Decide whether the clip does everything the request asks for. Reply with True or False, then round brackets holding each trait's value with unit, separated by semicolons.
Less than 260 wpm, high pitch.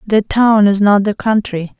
True (200 wpm; 205 Hz)